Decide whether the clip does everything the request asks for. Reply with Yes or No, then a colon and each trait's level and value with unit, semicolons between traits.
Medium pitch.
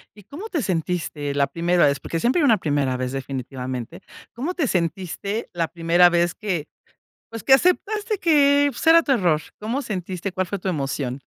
Yes: medium, 180 Hz